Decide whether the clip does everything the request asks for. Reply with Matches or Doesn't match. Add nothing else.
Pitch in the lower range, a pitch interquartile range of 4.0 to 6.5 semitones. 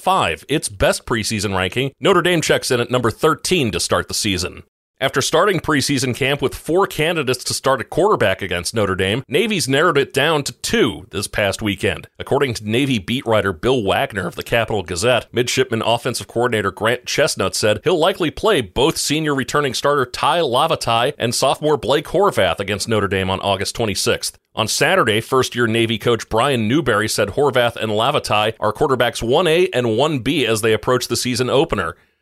Matches